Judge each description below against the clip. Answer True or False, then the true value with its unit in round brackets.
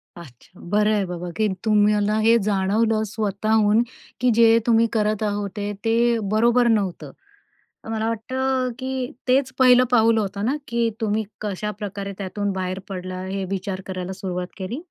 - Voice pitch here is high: True (210 Hz)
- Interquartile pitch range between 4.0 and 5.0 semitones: False (2.8 semitones)